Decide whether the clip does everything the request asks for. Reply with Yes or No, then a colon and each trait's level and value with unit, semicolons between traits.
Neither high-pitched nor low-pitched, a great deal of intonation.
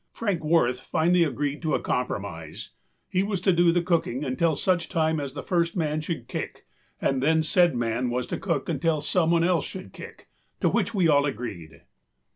No: medium, 160 Hz; average, 4.7 semitones